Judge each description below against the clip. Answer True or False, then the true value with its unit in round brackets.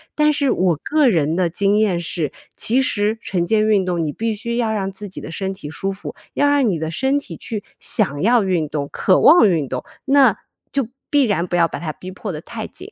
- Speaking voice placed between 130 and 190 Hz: False (200 Hz)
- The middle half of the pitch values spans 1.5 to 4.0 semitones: False (5.5 semitones)